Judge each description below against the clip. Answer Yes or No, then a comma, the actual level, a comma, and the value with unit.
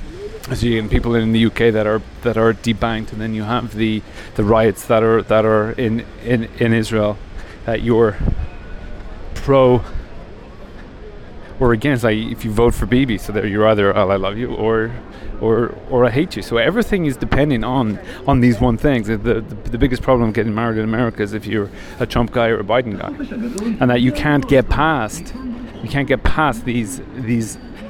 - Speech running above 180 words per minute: Yes, average, 200 wpm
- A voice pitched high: No, low, 115 Hz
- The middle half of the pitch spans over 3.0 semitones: No, average, 2.7 semitones